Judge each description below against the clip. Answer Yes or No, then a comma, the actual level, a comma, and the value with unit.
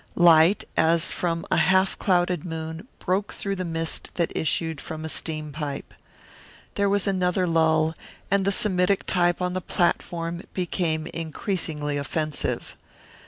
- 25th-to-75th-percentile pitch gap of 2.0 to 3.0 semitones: Yes, narrow, 2.5 semitones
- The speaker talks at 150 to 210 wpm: No, average, 140 wpm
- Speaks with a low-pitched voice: No, medium, 170 Hz